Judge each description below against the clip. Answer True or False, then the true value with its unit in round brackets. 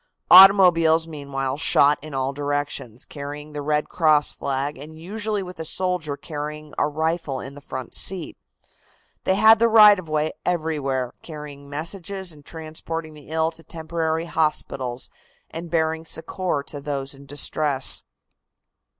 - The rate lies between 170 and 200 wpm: False (145 wpm)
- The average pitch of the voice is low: False (155 Hz)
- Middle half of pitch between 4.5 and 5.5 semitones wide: False (2.7 semitones)